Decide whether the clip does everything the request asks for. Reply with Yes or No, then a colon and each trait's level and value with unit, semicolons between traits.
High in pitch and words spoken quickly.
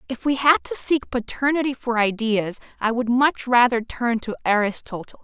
No: high, 240 Hz; average, 170 wpm